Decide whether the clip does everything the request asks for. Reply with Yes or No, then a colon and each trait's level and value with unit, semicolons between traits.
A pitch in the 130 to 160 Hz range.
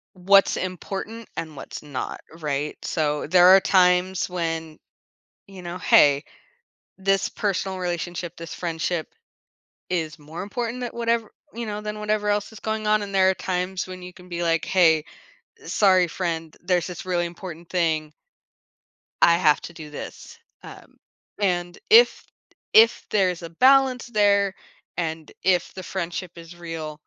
No: medium, 180 Hz